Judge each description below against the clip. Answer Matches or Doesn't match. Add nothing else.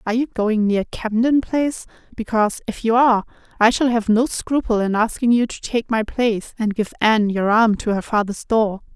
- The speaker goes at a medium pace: Doesn't match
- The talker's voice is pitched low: Doesn't match